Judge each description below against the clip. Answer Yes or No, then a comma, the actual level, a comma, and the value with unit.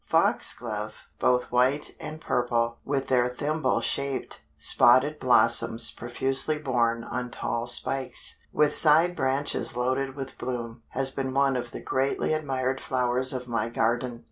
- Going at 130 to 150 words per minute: Yes, average, 140 wpm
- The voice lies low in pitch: Yes, low, 130 Hz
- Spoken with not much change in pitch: Yes, narrow, 2.1 semitones